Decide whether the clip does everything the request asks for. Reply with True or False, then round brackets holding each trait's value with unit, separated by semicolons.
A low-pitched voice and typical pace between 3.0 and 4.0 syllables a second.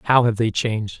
False (110 Hz; 5.3 syllables/s)